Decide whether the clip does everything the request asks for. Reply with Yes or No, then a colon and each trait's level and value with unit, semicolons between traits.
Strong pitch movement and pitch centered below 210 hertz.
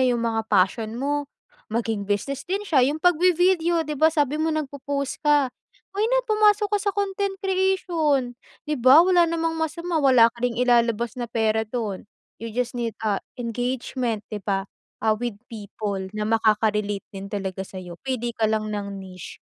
No: wide, 6.8 semitones; high, 245 Hz